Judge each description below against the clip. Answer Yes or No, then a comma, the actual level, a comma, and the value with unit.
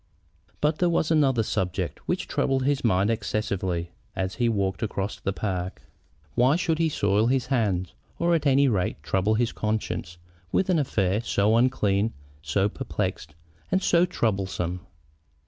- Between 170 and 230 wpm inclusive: No, average, 150 wpm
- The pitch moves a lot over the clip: Yes, wide, 5.9 semitones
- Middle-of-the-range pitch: No, low, 110 Hz